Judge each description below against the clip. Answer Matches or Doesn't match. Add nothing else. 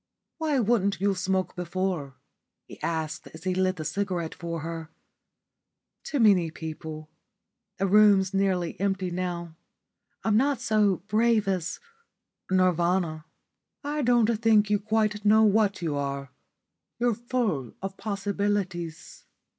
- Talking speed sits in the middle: Doesn't match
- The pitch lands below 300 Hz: Matches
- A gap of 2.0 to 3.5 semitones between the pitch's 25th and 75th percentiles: Doesn't match